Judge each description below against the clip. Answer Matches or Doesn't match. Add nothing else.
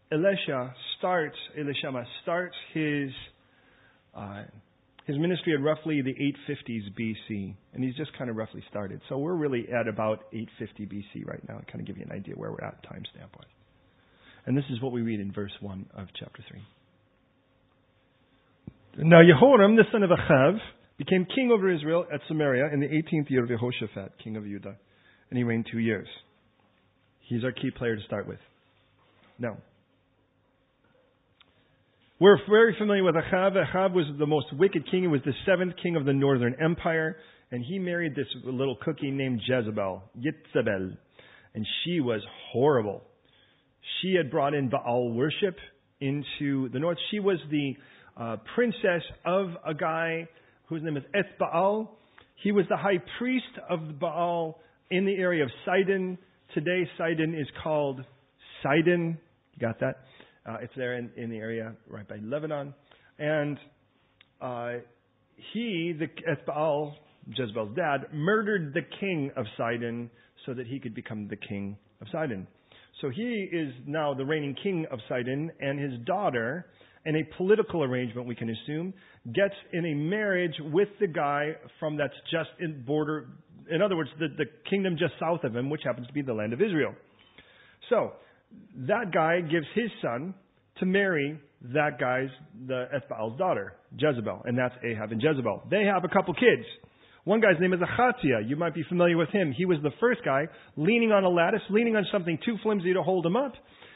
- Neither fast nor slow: Matches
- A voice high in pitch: Doesn't match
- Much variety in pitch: Matches